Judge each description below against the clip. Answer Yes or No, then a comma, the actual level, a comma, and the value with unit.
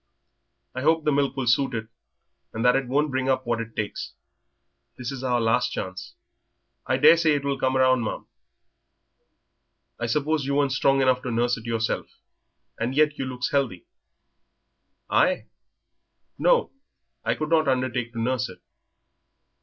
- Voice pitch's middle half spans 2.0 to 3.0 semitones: Yes, average, 2.7 semitones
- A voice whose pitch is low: Yes, low, 130 Hz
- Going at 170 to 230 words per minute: No, average, 160 wpm